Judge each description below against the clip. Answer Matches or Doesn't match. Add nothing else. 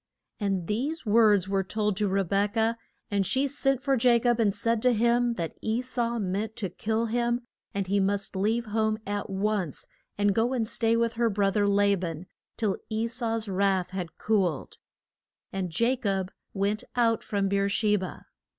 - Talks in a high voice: Matches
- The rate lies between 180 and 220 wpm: Matches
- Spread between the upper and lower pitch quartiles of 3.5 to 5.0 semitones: Doesn't match